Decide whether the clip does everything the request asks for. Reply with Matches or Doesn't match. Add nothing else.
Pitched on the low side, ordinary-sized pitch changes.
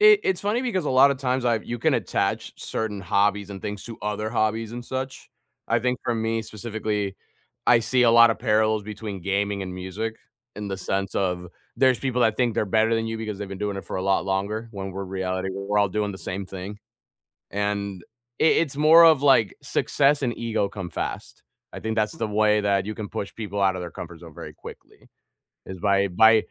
Matches